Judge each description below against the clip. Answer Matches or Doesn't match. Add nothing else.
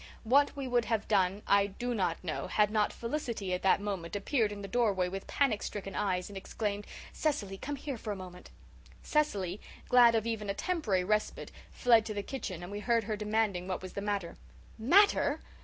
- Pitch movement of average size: Matches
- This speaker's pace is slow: Doesn't match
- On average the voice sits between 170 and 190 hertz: Doesn't match